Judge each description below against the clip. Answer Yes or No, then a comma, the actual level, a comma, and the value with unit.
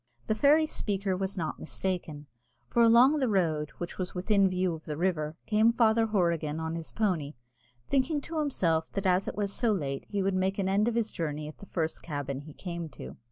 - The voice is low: No, medium, 185 Hz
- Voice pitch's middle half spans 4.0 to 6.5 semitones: Yes, average, 5.1 semitones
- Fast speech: Yes, fast, 210 wpm